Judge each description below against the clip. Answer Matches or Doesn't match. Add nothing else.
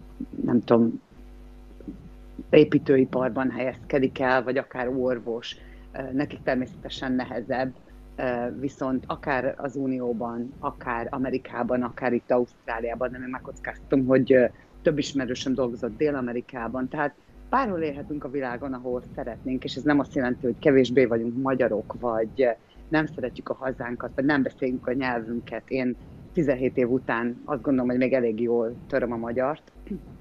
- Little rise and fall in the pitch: Matches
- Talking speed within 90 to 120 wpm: Doesn't match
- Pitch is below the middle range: Matches